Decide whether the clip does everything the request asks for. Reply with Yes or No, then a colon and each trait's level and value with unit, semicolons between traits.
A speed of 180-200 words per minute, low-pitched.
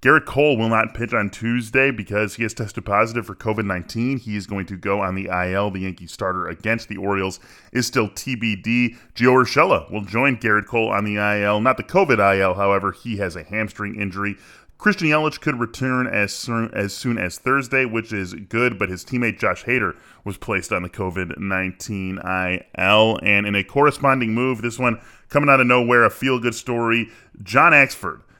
Yes: average, 195 wpm; low, 110 Hz